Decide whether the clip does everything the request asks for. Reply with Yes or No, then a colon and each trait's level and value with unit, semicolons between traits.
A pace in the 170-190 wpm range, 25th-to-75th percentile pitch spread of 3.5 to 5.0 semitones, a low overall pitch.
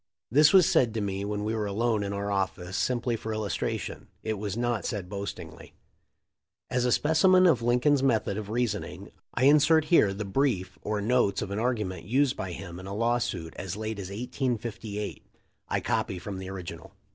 Yes: average, 185 wpm; average, 3.8 semitones; low, 110 Hz